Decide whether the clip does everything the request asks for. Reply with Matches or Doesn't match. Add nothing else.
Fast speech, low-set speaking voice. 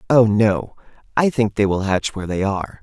Matches